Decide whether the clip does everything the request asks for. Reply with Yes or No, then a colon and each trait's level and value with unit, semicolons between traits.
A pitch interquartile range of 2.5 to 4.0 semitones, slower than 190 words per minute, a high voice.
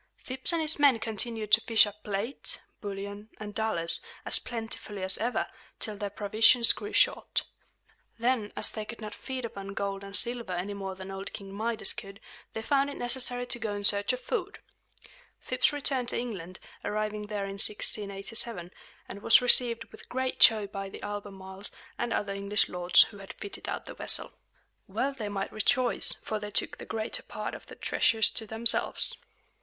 Yes: average, 3.3 semitones; average, 180 wpm; high, 215 Hz